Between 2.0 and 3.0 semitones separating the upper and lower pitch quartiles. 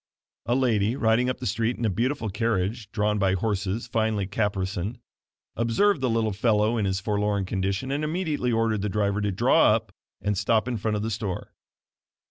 Yes: narrow, 2.6 semitones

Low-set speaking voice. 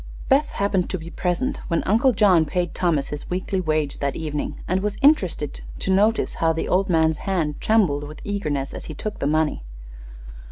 No: medium, 175 Hz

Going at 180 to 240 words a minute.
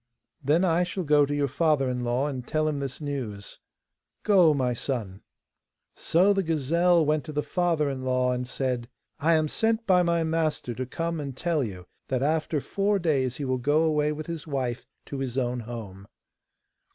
Yes: average, 190 wpm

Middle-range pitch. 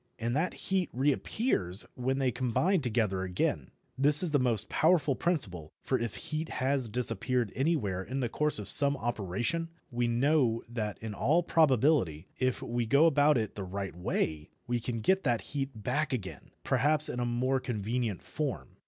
No: low, 125 Hz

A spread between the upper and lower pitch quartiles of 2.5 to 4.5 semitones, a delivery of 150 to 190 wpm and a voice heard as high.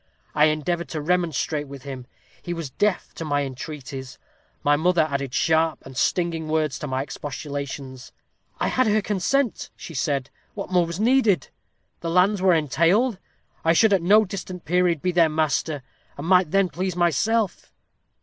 No: average, 4.0 semitones; average, 165 wpm; medium, 165 Hz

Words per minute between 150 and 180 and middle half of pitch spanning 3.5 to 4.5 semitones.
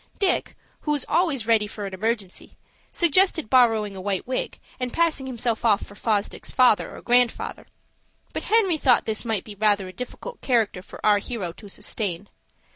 Yes: average, 175 wpm; average, 4.2 semitones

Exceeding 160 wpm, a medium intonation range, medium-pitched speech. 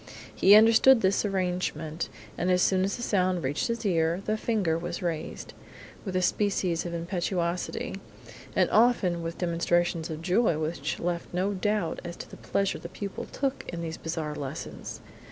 Yes: average, 170 wpm; average, 3.0 semitones; medium, 180 Hz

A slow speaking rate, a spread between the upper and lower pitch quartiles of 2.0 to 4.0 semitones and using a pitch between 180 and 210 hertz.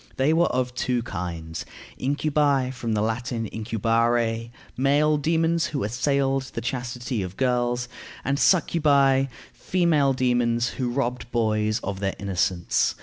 No: slow, 130 wpm; average, 3.5 semitones; low, 125 Hz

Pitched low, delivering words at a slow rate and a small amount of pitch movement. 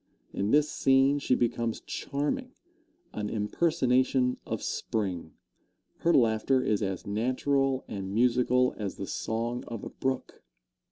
No: low, 125 Hz; slow, 125 wpm; average, 3.8 semitones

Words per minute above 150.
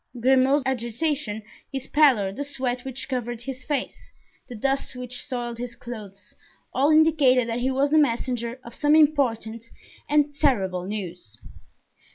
No: average, 145 wpm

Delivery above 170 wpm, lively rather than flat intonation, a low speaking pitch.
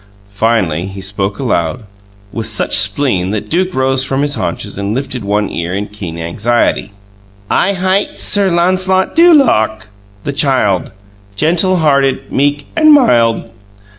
No: average, 140 wpm; wide, 8.7 semitones; low, 120 Hz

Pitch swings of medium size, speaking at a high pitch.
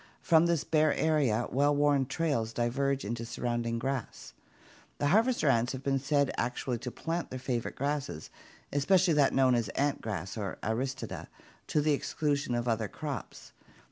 No: average, 3.7 semitones; low, 135 Hz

